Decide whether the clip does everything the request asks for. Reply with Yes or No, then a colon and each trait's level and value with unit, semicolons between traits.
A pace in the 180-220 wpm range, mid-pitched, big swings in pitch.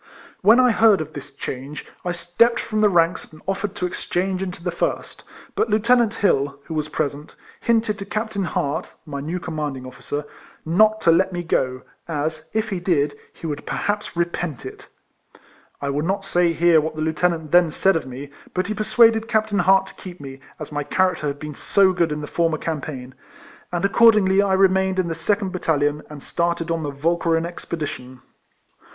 No: average, 195 wpm; medium, 170 Hz; average, 4.5 semitones